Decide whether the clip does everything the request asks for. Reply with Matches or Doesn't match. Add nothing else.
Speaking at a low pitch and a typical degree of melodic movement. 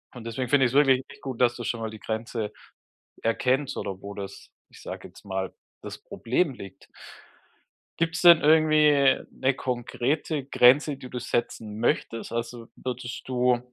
Matches